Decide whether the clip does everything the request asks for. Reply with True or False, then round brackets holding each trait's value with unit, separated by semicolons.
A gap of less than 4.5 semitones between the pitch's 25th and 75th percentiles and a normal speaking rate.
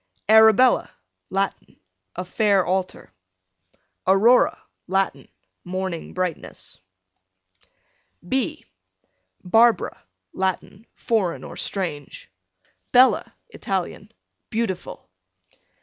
False (3.5 semitones; 70 wpm)